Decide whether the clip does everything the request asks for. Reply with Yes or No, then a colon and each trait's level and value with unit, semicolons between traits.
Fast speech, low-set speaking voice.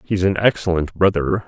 No: average, 165 wpm; very low, 95 Hz